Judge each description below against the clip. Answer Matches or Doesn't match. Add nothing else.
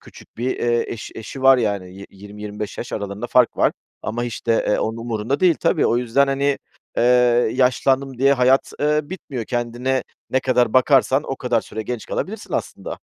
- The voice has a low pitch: Matches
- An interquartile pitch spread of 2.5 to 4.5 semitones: Matches